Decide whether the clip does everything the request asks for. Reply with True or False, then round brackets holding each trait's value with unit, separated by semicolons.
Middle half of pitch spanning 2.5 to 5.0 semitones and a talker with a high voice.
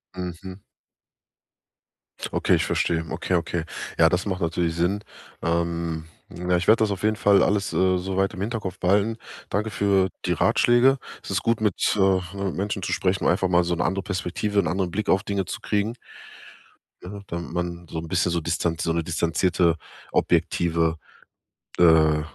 False (2.8 semitones; 90 Hz)